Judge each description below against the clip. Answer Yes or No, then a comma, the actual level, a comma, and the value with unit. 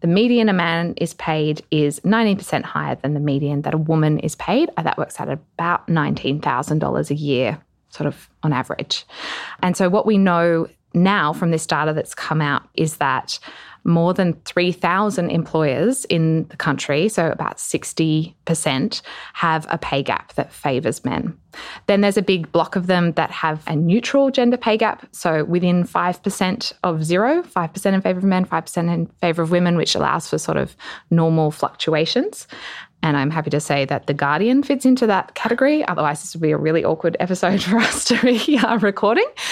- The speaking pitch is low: No, medium, 170 Hz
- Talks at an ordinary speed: Yes, average, 185 wpm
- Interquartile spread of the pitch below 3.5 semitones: No, average, 4.2 semitones